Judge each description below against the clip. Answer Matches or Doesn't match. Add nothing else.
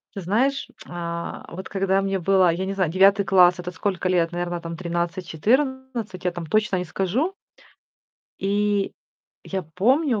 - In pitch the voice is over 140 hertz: Matches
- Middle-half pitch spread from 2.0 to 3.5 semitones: Matches